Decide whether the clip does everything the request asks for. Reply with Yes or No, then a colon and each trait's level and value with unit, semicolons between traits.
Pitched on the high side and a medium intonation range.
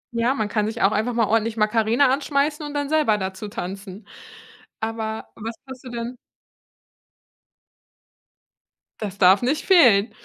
Yes: high, 225 Hz; average, 3.4 semitones